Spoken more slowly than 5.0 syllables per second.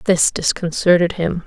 Yes: 4.5 syllables/s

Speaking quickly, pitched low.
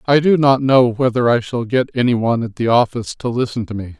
Yes: fast, 255 wpm; low, 120 Hz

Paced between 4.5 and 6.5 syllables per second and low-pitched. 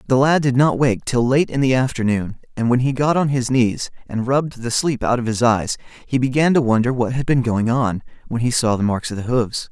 Yes: 5.3 syllables/s; low, 125 Hz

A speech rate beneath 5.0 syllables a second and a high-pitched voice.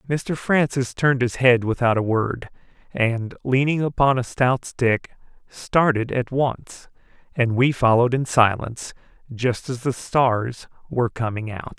No: 4.2 syllables/s; low, 125 Hz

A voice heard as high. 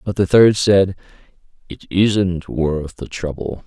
No: very low, 90 Hz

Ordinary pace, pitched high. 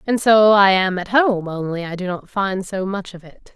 No: fast, 235 wpm; high, 195 Hz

